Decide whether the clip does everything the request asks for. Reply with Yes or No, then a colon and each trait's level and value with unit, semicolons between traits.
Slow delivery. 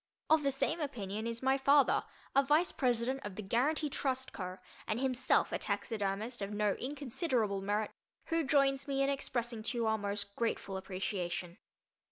No: average, 170 wpm